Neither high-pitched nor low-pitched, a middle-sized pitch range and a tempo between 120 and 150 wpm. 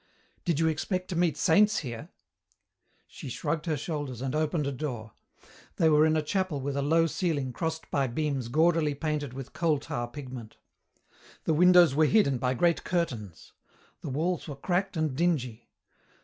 No: medium, 150 Hz; average, 3.9 semitones; average, 170 wpm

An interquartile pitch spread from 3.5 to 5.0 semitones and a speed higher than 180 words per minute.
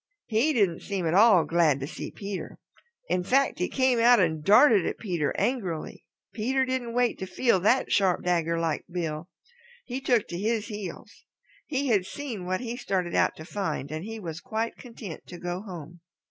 No: wide, 5.5 semitones; average, 190 wpm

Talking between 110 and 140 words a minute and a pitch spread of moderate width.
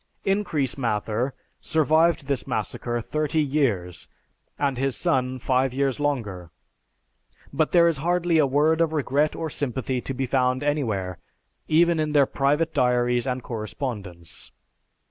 Yes: slow, 135 wpm; average, 3.9 semitones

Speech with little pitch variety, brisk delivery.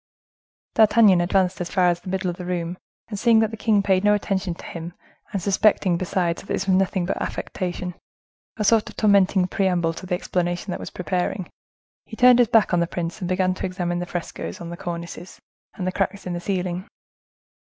Yes: narrow, 2.3 semitones; fast, 210 wpm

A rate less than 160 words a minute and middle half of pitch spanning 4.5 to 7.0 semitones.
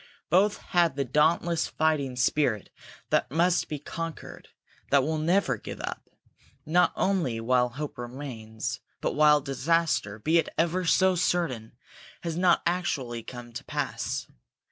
Yes: average, 140 wpm; wide, 5.4 semitones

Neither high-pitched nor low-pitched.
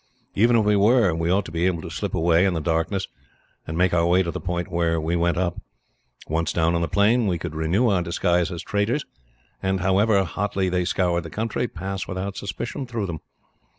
No: very low, 90 Hz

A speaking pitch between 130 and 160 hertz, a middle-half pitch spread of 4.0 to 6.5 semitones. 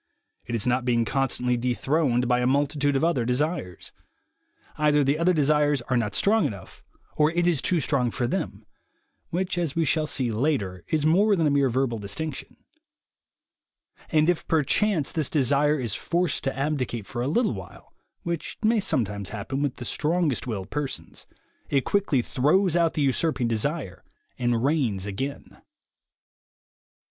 Yes: medium, 140 Hz; average, 4.5 semitones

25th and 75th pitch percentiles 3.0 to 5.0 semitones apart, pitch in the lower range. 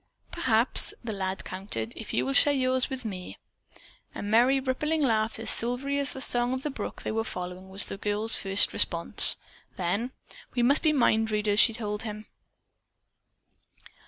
No: average, 4.2 semitones; high, 225 Hz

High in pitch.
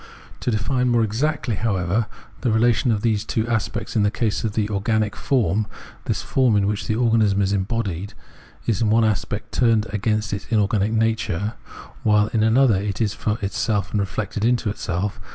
No: low, 110 Hz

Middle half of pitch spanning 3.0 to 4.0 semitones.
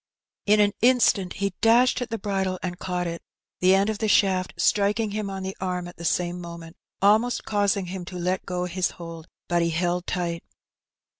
No: narrow, 2.6 semitones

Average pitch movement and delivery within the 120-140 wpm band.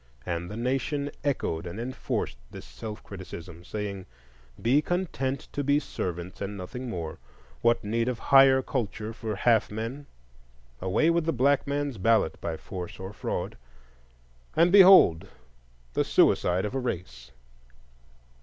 No: wide, 7.4 semitones; slow, 135 wpm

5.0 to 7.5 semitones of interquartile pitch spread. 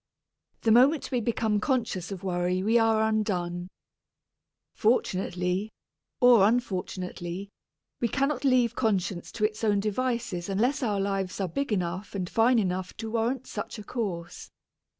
No: average, 4.2 semitones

